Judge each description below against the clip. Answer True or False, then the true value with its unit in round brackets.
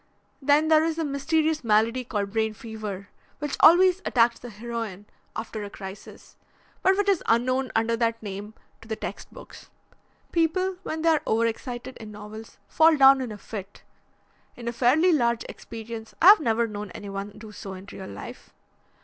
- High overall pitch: True (230 Hz)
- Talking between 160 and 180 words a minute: True (175 wpm)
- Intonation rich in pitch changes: True (5.7 semitones)